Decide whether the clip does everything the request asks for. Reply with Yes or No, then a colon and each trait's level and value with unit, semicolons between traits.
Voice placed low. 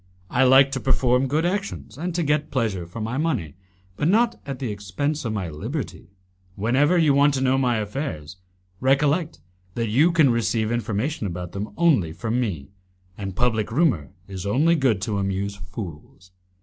Yes: low, 120 Hz